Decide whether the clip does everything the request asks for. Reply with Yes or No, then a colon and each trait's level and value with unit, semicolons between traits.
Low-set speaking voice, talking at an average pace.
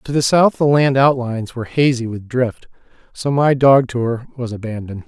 Yes: low, 125 Hz; average, 190 wpm